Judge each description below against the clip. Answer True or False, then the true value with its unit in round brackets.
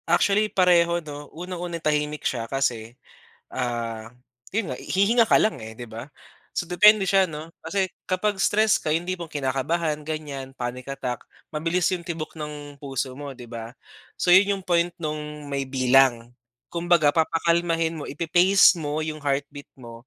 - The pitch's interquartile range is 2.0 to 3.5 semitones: False (4.4 semitones)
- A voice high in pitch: False (155 Hz)